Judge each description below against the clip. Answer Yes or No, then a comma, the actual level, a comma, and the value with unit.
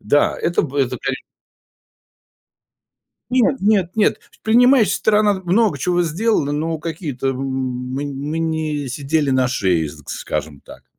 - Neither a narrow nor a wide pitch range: No, wide, 6.0 semitones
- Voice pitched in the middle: Yes, medium, 155 Hz